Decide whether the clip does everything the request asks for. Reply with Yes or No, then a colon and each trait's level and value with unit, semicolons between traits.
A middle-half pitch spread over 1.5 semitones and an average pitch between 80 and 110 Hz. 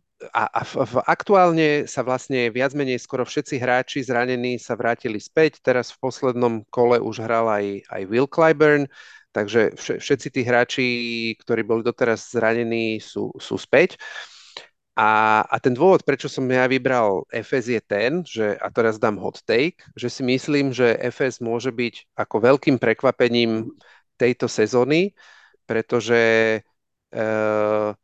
No: average, 2.8 semitones; low, 125 Hz